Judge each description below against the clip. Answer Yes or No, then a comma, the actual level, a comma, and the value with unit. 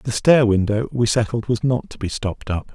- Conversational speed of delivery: No, fast, 240 wpm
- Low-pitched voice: Yes, low, 115 Hz